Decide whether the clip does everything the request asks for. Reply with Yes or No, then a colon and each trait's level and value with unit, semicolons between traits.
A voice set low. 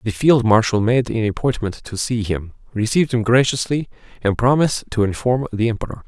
Yes: low, 115 Hz